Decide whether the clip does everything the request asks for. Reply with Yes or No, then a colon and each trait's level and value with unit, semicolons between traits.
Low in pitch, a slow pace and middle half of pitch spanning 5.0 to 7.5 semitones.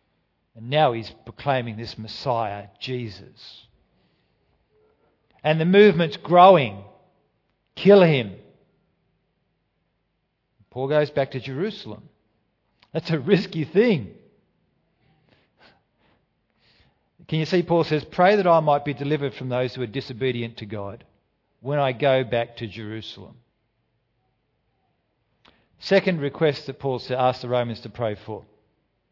Yes: low, 130 Hz; slow, 115 wpm; wide, 5.4 semitones